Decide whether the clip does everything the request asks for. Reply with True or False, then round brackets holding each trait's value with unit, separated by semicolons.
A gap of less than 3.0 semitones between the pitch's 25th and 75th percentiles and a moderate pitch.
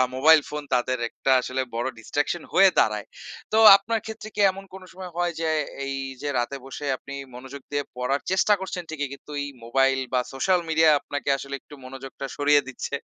False (4.8 semitones; 145 Hz)